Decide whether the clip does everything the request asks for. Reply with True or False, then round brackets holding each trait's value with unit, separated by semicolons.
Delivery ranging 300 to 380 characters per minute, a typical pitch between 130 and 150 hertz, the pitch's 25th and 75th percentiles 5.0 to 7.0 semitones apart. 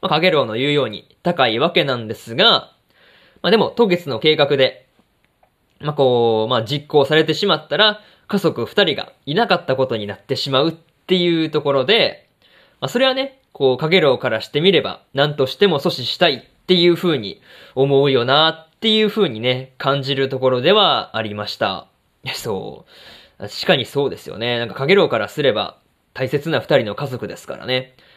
True (360 characters per minute; 140 Hz; 5.3 semitones)